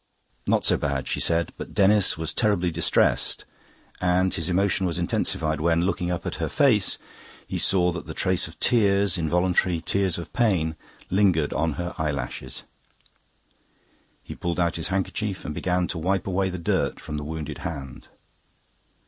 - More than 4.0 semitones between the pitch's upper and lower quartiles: No, average, 2.9 semitones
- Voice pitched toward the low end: Yes, very low, 90 Hz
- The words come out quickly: No, average, 165 wpm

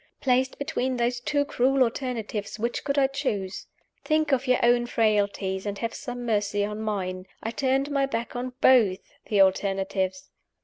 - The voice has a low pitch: No, high, 240 Hz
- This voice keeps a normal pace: Yes, average, 165 wpm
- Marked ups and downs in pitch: No, average, 4.4 semitones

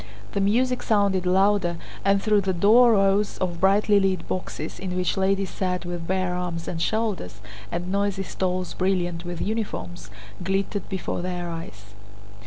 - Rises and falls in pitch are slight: Yes, narrow, 2.2 semitones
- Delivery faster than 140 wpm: Yes, average, 155 wpm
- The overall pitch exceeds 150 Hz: Yes, high, 190 Hz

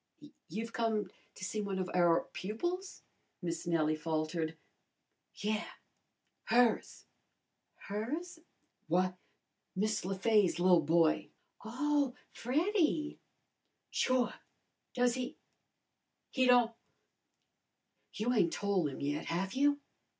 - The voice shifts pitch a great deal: Yes, wide, 6.2 semitones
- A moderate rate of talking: No, slow, 100 wpm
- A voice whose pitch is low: No, high, 210 Hz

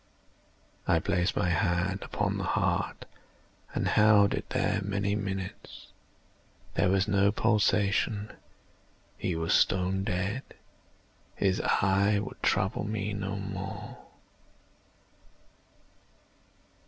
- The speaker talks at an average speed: No, slow, 100 wpm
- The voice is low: Yes, low, 100 Hz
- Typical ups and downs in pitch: No, narrow, 1.4 semitones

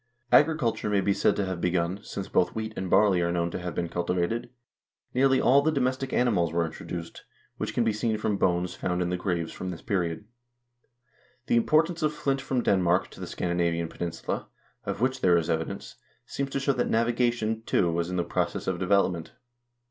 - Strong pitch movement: Yes, wide, 5.7 semitones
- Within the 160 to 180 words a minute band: No, average, 200 wpm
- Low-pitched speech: Yes, very low, 95 Hz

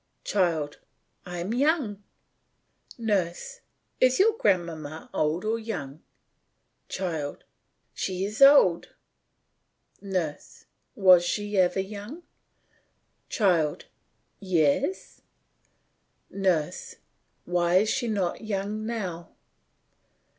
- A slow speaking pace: Yes, slow, 85 wpm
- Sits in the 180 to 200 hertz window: Yes, high, 190 Hz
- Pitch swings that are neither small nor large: Yes, average, 4.1 semitones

